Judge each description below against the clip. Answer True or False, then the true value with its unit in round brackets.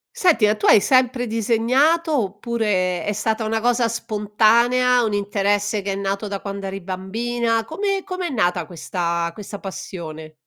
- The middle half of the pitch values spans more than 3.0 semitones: True (3.5 semitones)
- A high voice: True (215 Hz)